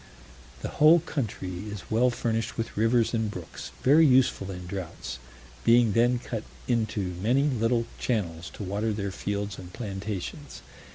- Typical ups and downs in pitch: Yes, average, 3.7 semitones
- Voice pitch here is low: Yes, low, 110 Hz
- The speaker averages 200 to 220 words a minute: No, average, 150 wpm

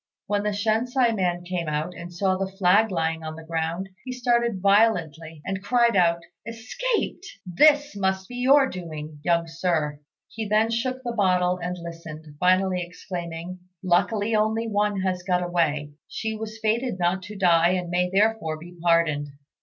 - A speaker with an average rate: Yes, average, 165 wpm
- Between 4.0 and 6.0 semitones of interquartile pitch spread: Yes, average, 4.4 semitones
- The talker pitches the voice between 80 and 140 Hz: No, medium, 185 Hz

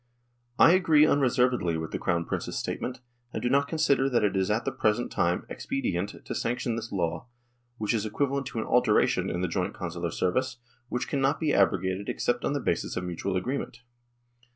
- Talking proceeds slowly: No, average, 190 wpm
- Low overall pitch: Yes, low, 115 Hz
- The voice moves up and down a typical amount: No, wide, 6.6 semitones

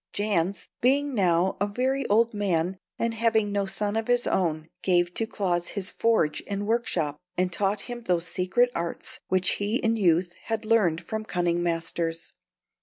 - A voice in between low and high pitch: No, high, 200 Hz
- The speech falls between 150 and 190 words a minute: Yes, average, 170 wpm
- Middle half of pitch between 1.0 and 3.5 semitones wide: No, average, 4.5 semitones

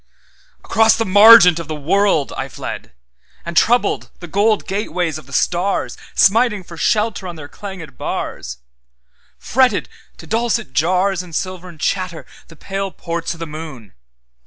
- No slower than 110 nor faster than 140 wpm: Yes, slow, 135 wpm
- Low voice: No, medium, 175 Hz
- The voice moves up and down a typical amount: Yes, average, 4.6 semitones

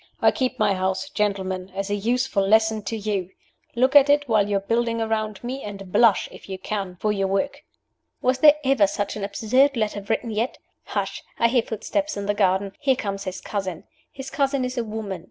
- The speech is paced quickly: Yes, fast, 210 wpm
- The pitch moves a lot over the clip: No, average, 4.1 semitones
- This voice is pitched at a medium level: No, high, 215 Hz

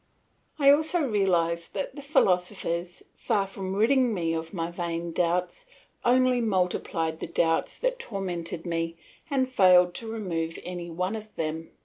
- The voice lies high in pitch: No, medium, 180 Hz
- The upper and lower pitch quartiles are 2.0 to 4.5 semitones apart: No, average, 5.2 semitones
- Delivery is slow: No, average, 145 wpm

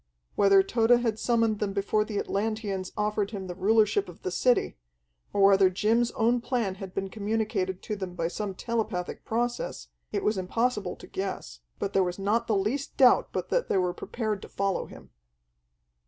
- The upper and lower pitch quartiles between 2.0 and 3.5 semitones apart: Yes, average, 2.7 semitones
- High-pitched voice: Yes, high, 205 Hz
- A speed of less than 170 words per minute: No, average, 185 wpm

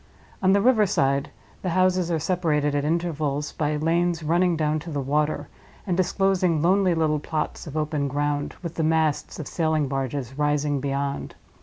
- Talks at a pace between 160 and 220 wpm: Yes, average, 170 wpm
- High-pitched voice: No, medium, 155 Hz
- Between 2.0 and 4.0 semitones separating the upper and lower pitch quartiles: Yes, average, 3.1 semitones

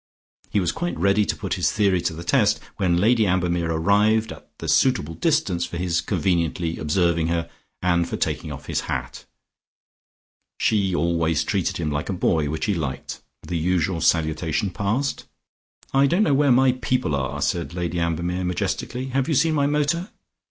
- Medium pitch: No, very low, 90 Hz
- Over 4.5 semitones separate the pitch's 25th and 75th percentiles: Yes, average, 5.0 semitones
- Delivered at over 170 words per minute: Yes, average, 180 wpm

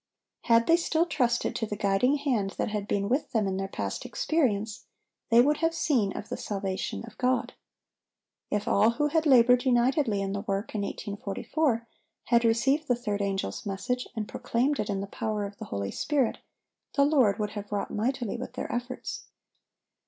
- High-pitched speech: Yes, high, 230 Hz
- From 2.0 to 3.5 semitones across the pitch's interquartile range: No, average, 4.5 semitones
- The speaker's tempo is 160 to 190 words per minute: Yes, average, 185 wpm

